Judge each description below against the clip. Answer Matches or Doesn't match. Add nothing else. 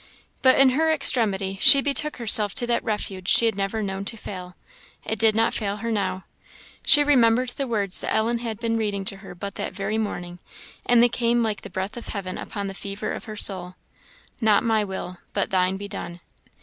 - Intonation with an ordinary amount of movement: Matches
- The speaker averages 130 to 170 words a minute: Doesn't match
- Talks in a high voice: Matches